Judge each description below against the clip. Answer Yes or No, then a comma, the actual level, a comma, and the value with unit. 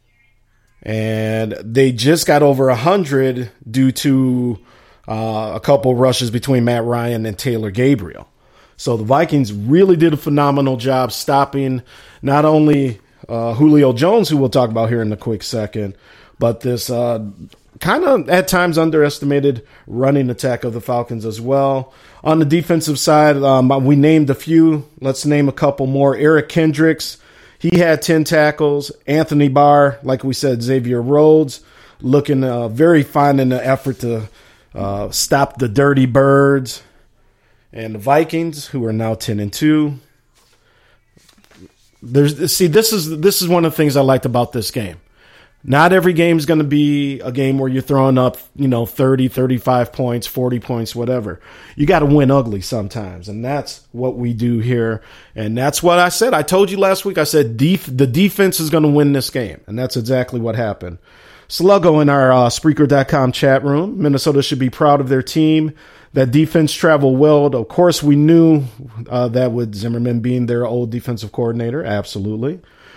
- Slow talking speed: No, average, 175 wpm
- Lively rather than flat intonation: No, average, 3.8 semitones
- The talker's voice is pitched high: No, low, 135 Hz